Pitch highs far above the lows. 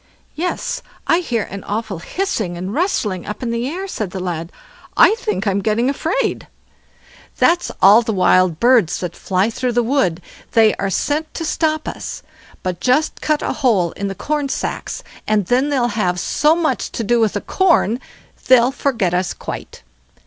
Yes: wide, 6.9 semitones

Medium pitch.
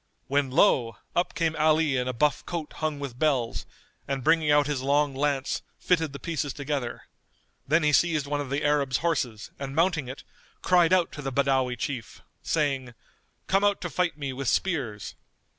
Yes: medium, 145 Hz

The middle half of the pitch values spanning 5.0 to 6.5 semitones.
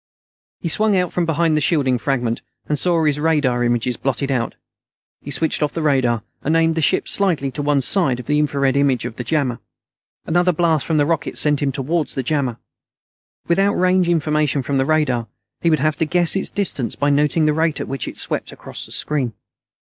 No: average, 3.4 semitones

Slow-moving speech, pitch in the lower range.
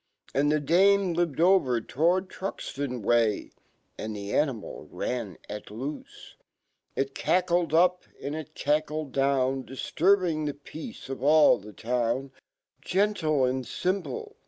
No: slow, 110 wpm; medium, 145 Hz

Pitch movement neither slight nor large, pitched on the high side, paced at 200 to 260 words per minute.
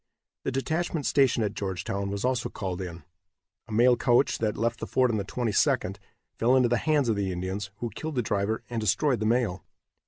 No: average, 4.3 semitones; low, 115 Hz; fast, 205 wpm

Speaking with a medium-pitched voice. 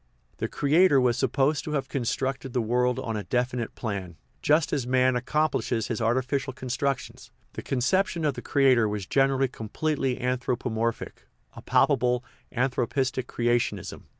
No: low, 130 Hz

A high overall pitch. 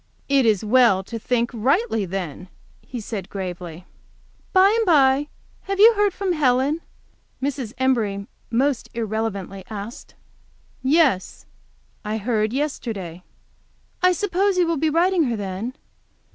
Yes: high, 245 Hz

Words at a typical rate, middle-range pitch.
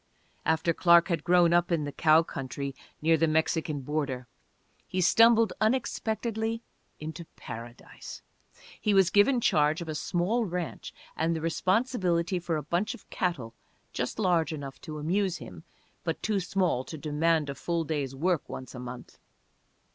Yes: average, 155 wpm; medium, 165 Hz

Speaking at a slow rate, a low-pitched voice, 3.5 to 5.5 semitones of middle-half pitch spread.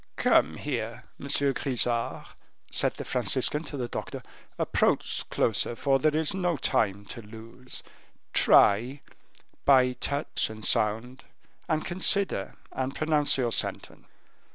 Yes: slow, 125 wpm; low, 130 Hz; average, 4.2 semitones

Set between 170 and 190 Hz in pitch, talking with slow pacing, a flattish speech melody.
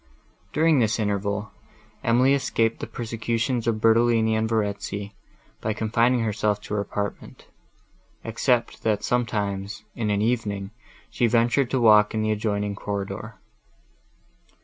No: low, 110 Hz; slow, 125 wpm; narrow, 2.1 semitones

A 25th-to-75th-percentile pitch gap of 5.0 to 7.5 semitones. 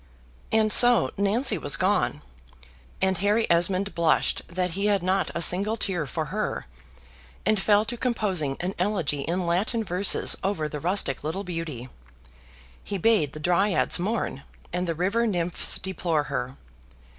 No: average, 3.7 semitones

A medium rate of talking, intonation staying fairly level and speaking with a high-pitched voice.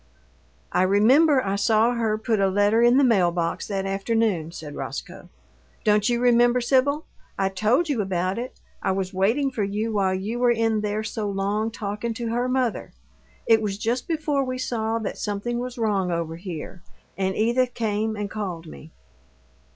No: average, 180 wpm; average, 3.6 semitones; high, 215 Hz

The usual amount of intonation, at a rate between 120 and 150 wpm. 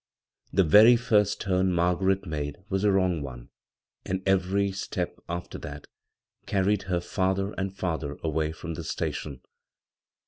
Yes: average, 3.5 semitones; average, 140 wpm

